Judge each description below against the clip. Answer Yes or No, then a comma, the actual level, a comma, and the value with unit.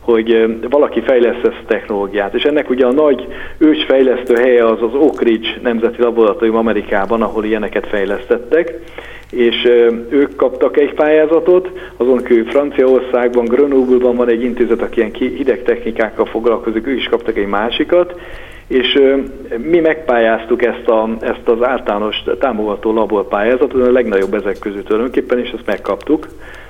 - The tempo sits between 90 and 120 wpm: No, average, 140 wpm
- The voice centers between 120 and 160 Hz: Yes, low, 125 Hz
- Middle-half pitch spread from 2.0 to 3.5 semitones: No, average, 4.2 semitones